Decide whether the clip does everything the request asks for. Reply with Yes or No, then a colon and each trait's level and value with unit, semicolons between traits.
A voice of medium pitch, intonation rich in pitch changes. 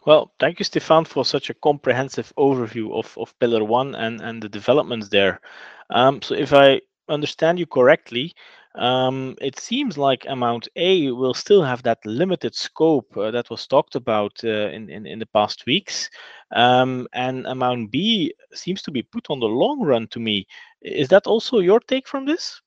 No: low, 130 Hz; wide, 6.1 semitones